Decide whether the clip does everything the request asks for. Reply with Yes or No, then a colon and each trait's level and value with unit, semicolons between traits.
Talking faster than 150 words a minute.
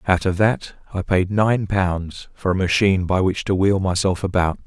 Yes: fast, 205 wpm